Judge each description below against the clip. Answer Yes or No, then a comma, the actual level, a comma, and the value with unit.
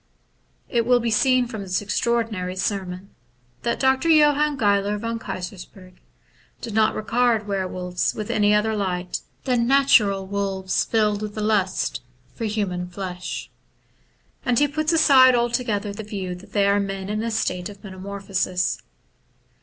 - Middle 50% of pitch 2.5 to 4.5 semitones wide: Yes, average, 3.6 semitones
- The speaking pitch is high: Yes, high, 210 Hz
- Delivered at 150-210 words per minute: Yes, average, 155 wpm